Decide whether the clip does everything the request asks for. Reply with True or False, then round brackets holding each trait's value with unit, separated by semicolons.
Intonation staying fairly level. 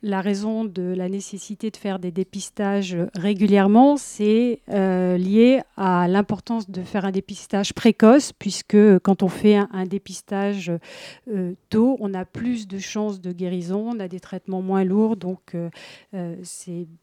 True (2.2 semitones)